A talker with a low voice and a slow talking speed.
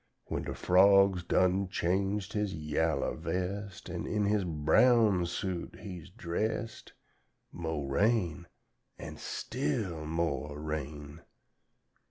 Yes: very low, 90 Hz; slow, 110 wpm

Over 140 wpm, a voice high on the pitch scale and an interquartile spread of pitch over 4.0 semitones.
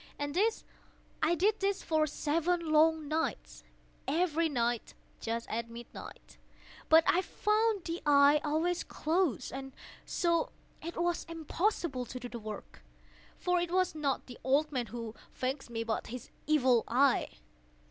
No: slow, 135 wpm; very high, 305 Hz; average, 5.2 semitones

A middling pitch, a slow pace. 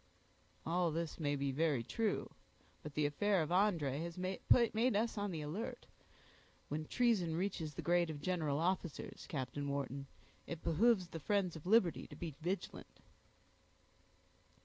No: medium, 170 Hz; average, 150 wpm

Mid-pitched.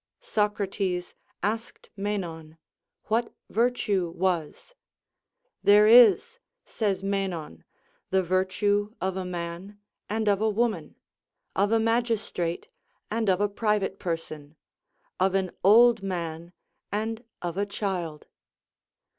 No: high, 200 Hz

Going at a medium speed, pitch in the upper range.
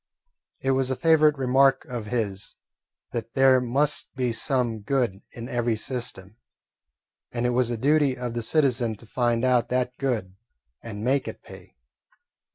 No: average, 160 wpm; low, 125 Hz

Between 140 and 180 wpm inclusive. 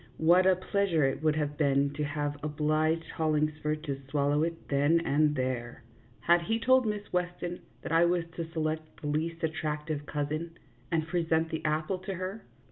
Yes: average, 175 wpm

